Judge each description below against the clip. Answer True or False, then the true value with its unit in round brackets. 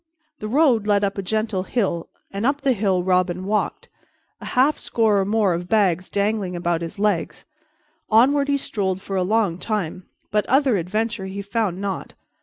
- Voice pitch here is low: False (200 Hz)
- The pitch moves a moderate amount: True (3.3 semitones)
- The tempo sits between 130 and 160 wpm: False (180 wpm)